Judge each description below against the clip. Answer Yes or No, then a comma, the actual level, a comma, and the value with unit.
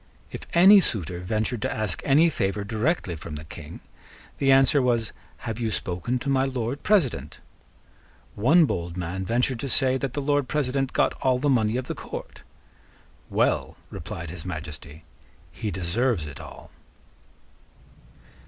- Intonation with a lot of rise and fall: Yes, wide, 7.0 semitones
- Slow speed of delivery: No, average, 155 wpm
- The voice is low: Yes, low, 115 Hz